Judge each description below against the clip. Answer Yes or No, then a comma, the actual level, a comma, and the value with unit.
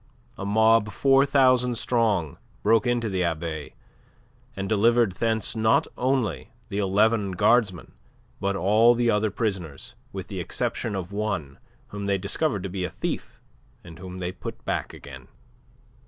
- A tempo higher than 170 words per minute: No, average, 150 wpm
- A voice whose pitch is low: Yes, low, 105 Hz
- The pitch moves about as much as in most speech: Yes, average, 3.7 semitones